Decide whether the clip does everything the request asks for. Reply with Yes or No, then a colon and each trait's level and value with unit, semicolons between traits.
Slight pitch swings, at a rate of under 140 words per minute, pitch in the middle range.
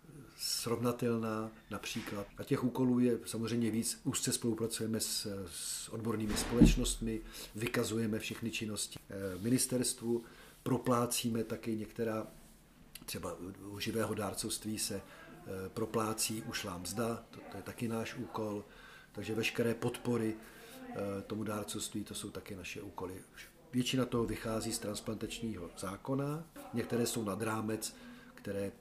No: narrow, 2.1 semitones; slow, 115 wpm; low, 110 Hz